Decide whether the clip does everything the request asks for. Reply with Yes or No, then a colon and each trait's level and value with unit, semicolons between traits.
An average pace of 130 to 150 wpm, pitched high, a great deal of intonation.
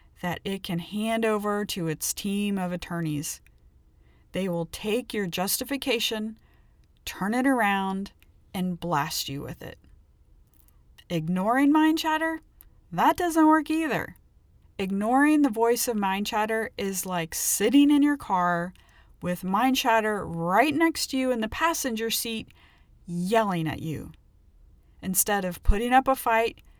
Yes: average, 140 wpm; high, 200 Hz; wide, 6.0 semitones